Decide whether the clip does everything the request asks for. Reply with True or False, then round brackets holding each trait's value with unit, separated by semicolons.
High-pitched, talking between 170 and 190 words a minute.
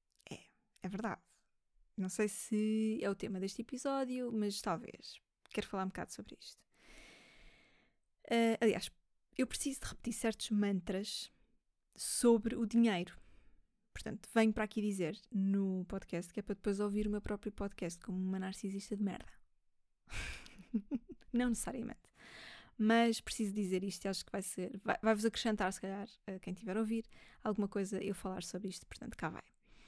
False (205 Hz; 160 wpm)